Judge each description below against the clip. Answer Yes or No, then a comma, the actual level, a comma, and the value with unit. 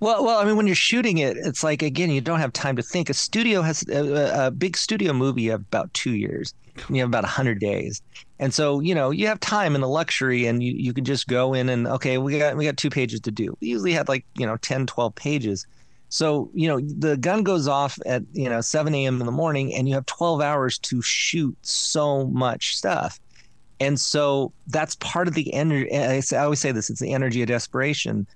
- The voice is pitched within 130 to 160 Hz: Yes, medium, 140 Hz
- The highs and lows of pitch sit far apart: No, average, 3.6 semitones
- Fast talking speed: Yes, fast, 235 wpm